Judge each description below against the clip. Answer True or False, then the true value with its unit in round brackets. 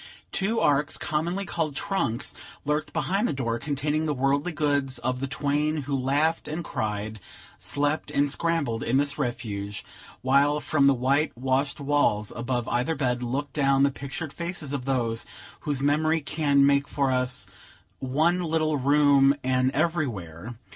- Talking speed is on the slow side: False (155 wpm)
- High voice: False (140 Hz)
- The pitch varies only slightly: False (3.0 semitones)